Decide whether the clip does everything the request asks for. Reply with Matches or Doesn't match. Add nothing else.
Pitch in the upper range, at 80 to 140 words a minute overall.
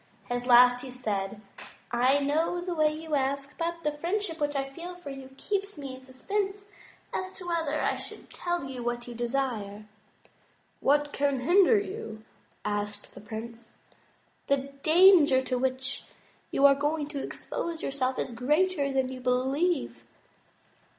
Doesn't match